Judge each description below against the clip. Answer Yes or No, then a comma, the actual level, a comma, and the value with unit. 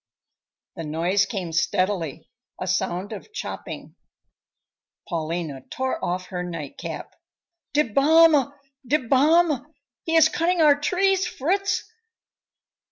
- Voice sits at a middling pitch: No, high, 245 Hz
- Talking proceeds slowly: Yes, slow, 110 wpm